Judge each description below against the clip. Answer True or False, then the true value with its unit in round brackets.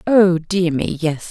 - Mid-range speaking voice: True (175 Hz)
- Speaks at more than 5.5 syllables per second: False (3.6 syllables/s)